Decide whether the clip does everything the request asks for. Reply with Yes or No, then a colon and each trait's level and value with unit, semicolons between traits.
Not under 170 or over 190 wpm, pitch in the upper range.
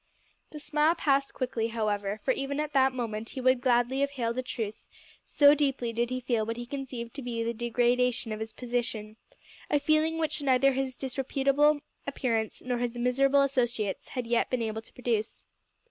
Yes: average, 185 wpm; very high, 250 Hz